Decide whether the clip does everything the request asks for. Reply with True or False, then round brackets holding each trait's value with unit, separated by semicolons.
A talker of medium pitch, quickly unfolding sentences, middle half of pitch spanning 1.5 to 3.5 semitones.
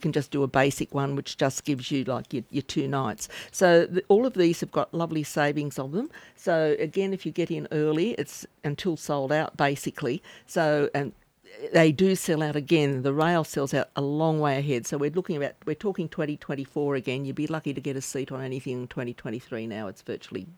True (150 Hz; 220 wpm; 3.1 semitones)